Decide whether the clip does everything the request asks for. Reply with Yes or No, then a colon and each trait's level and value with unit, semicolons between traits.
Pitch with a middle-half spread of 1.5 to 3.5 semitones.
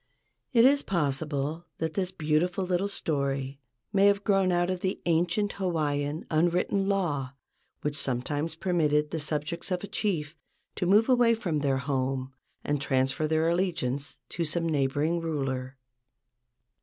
No: average, 4.2 semitones